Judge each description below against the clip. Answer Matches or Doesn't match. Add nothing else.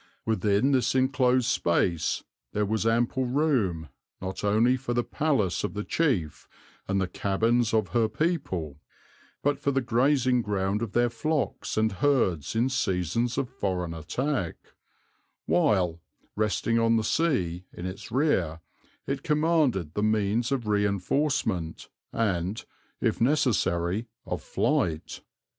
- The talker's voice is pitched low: Matches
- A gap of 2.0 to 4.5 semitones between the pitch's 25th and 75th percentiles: Doesn't match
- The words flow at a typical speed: Doesn't match